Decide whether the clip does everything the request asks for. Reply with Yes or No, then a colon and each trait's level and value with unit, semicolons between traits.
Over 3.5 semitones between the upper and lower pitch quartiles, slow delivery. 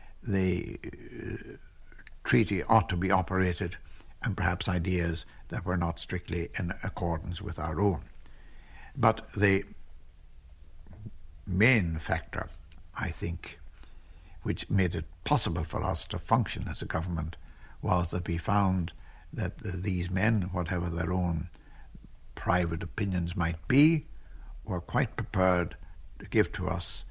No: average, 2.9 semitones; slow, 130 wpm